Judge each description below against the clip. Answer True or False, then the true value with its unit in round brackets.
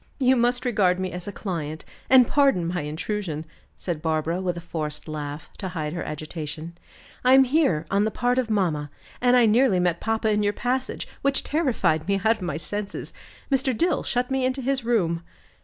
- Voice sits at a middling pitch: False (200 Hz)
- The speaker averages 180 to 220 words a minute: True (195 wpm)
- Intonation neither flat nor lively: False (7.3 semitones)